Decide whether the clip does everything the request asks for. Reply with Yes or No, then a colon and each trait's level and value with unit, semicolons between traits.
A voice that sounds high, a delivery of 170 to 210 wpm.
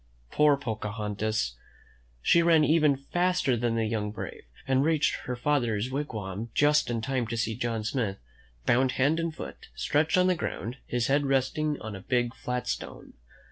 No: low, 125 Hz; average, 175 wpm